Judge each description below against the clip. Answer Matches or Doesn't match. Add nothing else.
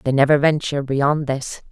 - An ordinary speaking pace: Matches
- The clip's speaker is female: Matches